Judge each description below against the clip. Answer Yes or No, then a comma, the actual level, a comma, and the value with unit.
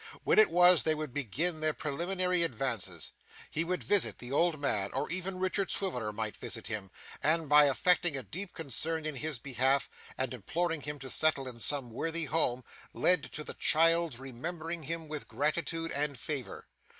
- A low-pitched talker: No, medium, 155 Hz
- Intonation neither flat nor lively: Yes, average, 4.3 semitones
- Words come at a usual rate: Yes, average, 175 wpm